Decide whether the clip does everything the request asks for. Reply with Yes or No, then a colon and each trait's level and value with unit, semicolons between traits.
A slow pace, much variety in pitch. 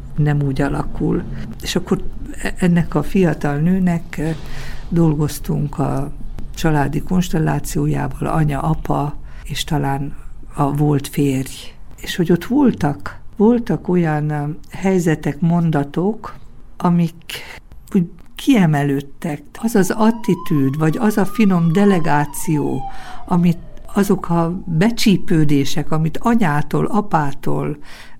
No: slow, 100 wpm; average, 4.0 semitones